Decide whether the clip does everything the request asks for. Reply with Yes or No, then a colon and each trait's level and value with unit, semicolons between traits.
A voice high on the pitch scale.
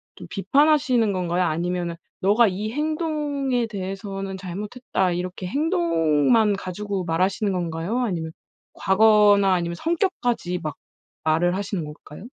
Yes: high, 195 Hz